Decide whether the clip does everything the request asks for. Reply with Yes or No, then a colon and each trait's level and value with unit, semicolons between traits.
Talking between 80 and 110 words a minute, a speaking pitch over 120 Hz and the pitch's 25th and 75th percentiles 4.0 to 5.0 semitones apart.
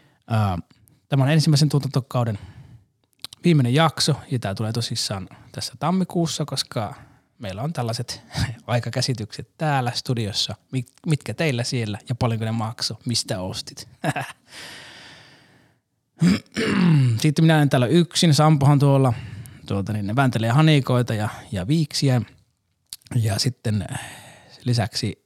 Yes: average, 105 wpm; low, 130 Hz; average, 4.4 semitones